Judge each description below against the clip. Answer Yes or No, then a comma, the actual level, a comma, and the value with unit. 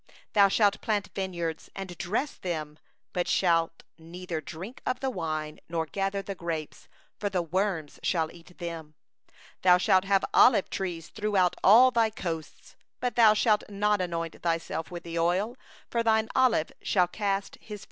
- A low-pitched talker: No, medium, 185 Hz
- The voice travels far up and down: No, average, 3.8 semitones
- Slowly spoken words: No, average, 165 wpm